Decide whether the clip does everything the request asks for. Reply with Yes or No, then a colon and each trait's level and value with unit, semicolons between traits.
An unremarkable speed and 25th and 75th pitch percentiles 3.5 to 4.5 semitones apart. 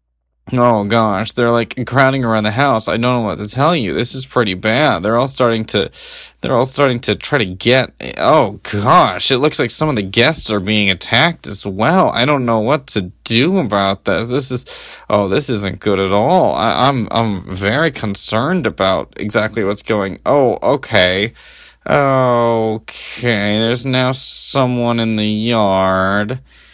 Yes: average, 175 wpm; average, 3.8 semitones